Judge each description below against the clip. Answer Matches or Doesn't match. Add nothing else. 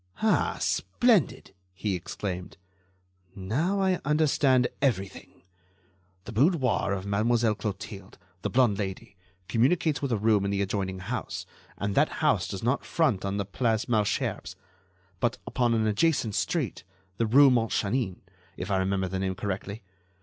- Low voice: Matches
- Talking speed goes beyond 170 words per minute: Doesn't match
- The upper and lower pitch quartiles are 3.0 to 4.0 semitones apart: Doesn't match